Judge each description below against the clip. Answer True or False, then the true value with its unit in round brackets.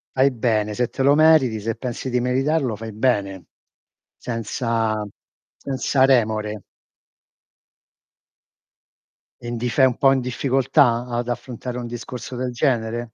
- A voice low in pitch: True (120 Hz)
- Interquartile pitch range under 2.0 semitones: False (2.7 semitones)